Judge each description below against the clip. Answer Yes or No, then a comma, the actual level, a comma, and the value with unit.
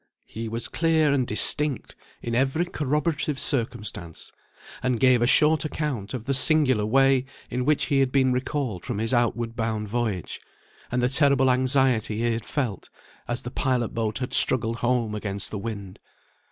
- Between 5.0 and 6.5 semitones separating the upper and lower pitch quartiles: No, average, 3.3 semitones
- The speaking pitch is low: Yes, low, 125 Hz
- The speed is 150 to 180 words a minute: Yes, average, 165 wpm